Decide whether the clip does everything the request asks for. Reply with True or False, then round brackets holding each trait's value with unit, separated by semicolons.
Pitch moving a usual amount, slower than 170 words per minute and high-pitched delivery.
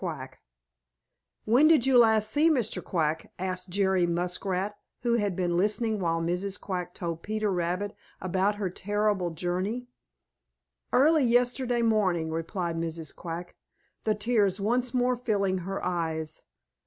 True (4.2 semitones; 135 wpm; 195 Hz)